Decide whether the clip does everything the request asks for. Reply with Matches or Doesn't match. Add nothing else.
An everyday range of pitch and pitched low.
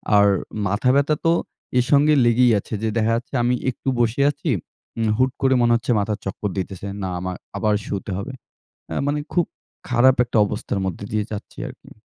Matches